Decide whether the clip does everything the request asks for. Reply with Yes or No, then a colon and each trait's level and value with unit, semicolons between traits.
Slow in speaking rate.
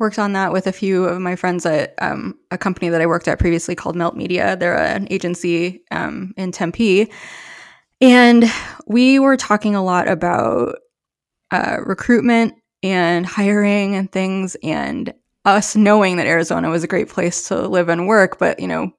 No: average, 175 wpm